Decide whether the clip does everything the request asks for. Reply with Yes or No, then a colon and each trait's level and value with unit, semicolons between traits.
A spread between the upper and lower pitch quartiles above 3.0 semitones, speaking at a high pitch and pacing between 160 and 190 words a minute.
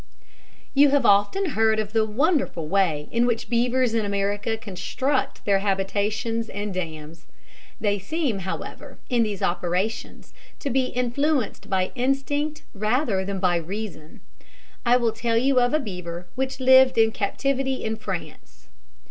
No: average, 4.8 semitones; high, 220 Hz; average, 145 wpm